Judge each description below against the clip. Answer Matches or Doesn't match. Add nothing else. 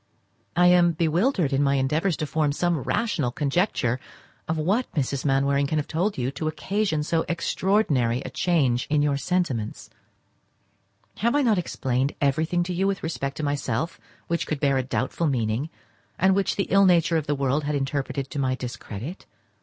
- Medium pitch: Matches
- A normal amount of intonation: Matches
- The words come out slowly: Doesn't match